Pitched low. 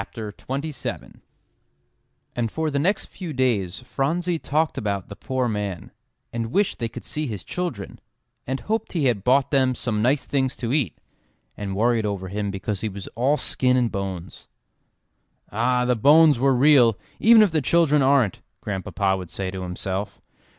Yes: low, 125 Hz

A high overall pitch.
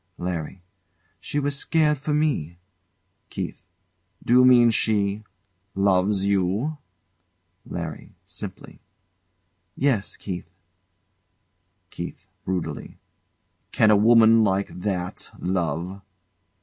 No: low, 100 Hz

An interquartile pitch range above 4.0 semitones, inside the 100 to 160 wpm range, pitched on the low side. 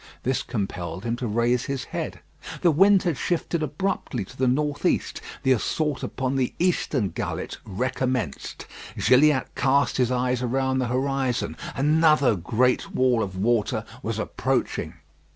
No: average, 3.0 semitones; average, 145 wpm; low, 130 Hz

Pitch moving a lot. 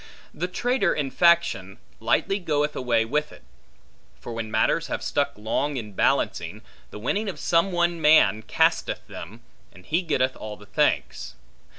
Yes: wide, 7.6 semitones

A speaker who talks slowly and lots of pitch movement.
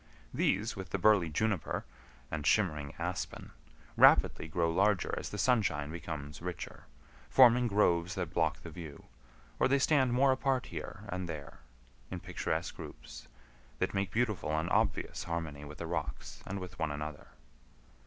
No: average, 155 wpm; wide, 5.7 semitones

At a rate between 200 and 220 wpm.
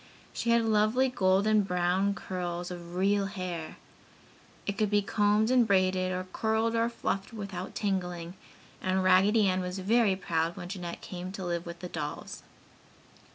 No: average, 155 wpm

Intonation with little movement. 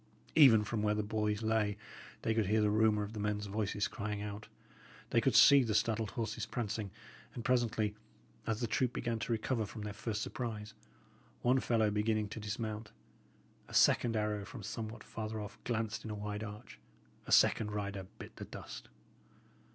Yes: narrow, 1.4 semitones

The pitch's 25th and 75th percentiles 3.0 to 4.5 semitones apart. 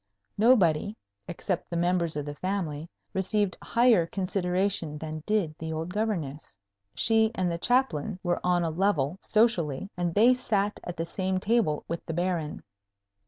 Yes: average, 4.2 semitones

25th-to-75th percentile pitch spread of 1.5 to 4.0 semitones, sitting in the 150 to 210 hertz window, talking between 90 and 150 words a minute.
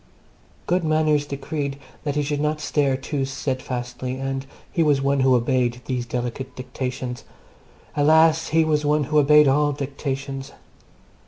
No: narrow, 2.4 semitones; medium, 140 Hz; average, 145 wpm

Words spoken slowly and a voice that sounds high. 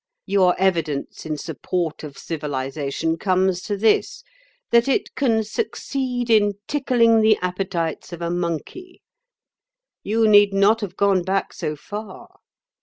Yes: slow, 125 wpm; high, 195 Hz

